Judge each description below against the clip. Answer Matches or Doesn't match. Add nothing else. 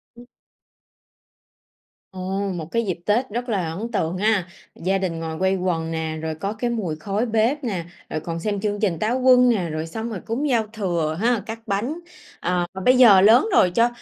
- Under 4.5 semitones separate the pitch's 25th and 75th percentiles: Doesn't match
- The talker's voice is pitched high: Matches